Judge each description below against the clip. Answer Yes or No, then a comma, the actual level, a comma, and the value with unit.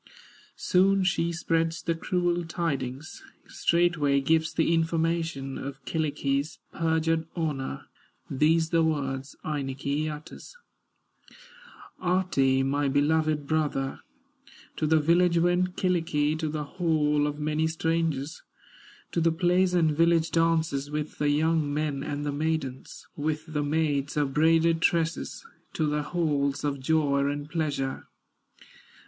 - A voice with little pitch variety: Yes, narrow, 2.3 semitones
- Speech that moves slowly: Yes, slow, 125 wpm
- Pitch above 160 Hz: No, medium, 155 Hz